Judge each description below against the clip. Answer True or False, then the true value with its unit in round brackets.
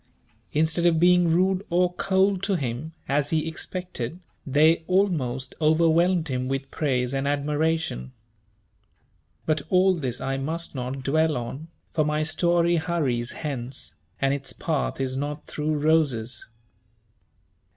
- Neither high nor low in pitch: True (155 Hz)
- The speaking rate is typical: False (130 wpm)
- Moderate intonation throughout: True (4.0 semitones)